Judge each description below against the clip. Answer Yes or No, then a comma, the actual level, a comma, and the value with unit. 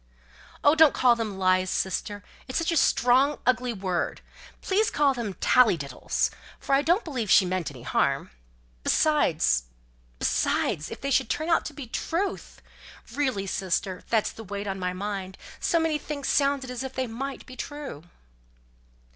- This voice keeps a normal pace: Yes, average, 165 wpm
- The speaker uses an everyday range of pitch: No, wide, 7.0 semitones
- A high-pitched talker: Yes, high, 245 Hz